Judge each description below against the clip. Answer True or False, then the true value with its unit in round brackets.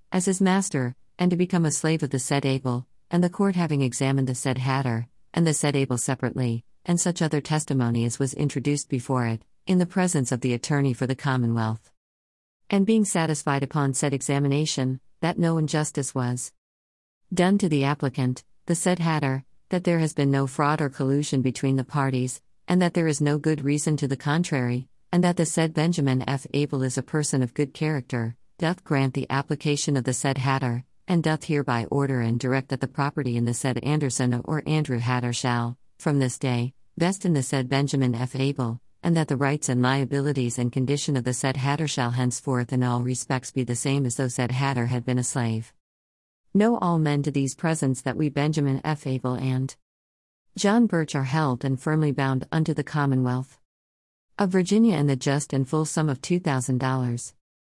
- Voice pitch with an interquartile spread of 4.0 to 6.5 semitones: False (3.4 semitones)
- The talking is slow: False (200 wpm)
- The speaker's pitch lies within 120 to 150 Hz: True (135 Hz)